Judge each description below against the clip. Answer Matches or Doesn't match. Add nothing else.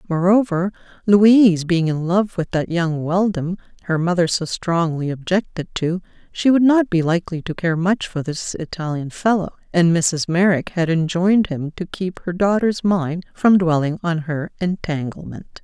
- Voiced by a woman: Matches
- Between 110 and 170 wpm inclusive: Matches